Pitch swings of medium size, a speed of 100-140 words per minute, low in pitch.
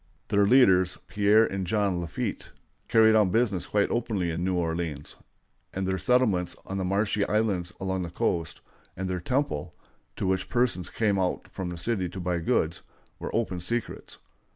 No: average, 3.4 semitones; average, 170 wpm; very low, 95 Hz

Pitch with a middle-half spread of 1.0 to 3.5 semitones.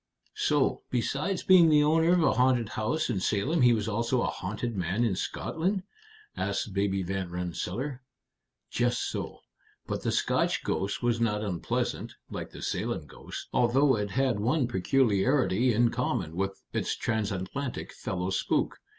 No: average, 5.3 semitones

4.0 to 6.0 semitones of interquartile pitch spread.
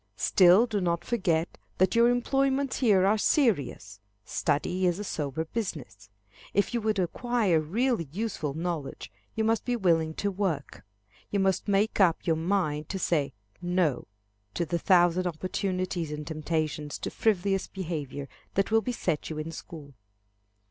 Yes: average, 4.6 semitones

